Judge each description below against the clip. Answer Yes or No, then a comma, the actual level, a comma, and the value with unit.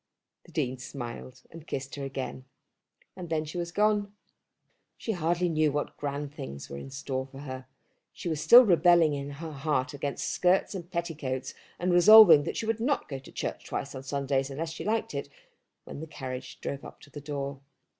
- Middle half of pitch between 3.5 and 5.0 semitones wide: Yes, average, 4.2 semitones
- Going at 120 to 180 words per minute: No, average, 195 wpm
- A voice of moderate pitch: Yes, medium, 145 Hz